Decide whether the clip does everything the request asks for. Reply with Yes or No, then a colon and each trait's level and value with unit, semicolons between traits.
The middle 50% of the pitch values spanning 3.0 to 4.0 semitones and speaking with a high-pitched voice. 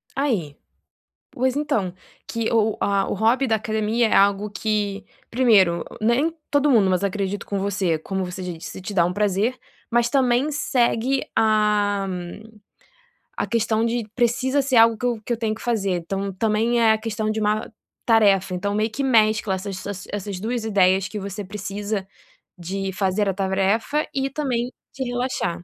Yes: average, 3.3 semitones; high, 215 Hz